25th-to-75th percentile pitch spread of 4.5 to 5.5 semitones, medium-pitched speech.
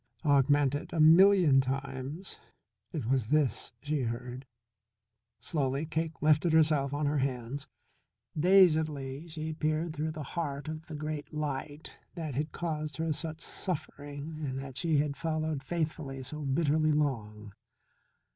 No: narrow, 2.5 semitones; medium, 150 Hz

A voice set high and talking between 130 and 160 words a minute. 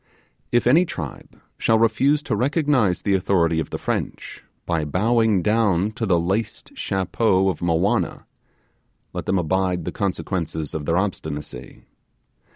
No: very low, 95 Hz; average, 140 wpm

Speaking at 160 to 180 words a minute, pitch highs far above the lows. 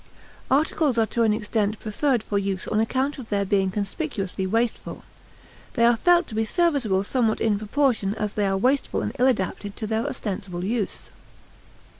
No: average, 175 wpm; average, 4.2 semitones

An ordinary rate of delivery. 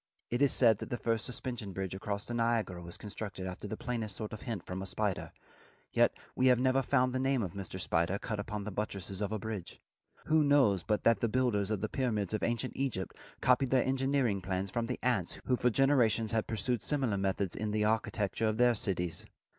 No: fast, 220 wpm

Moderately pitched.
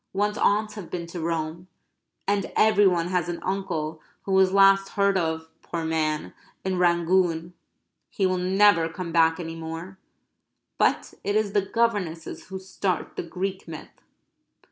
Yes: medium, 180 Hz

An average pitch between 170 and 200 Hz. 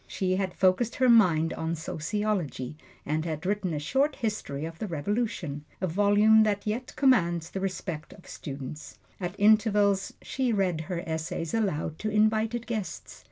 Yes: high, 190 Hz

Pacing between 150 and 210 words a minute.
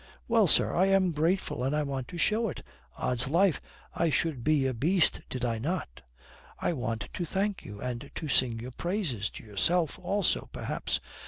Yes: average, 185 wpm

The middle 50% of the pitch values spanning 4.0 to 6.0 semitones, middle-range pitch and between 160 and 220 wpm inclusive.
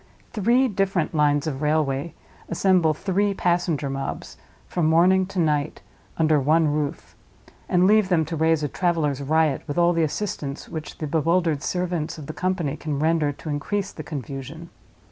No: average, 3.2 semitones; medium, 160 Hz; average, 165 wpm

